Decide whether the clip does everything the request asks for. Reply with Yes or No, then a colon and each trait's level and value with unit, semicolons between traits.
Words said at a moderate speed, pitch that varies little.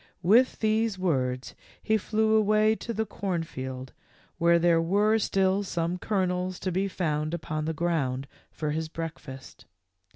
No: average, 150 wpm; average, 4.9 semitones